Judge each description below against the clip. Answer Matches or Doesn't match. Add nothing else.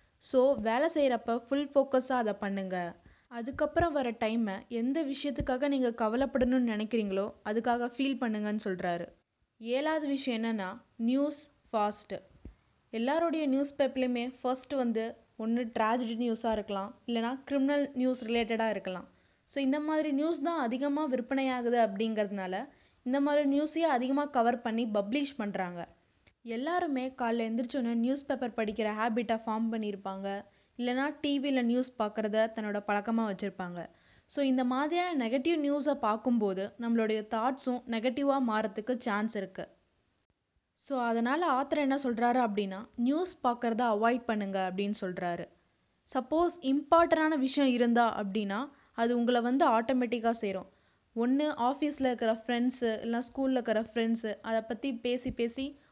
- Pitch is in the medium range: Doesn't match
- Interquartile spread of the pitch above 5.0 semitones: Doesn't match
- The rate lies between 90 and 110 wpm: Doesn't match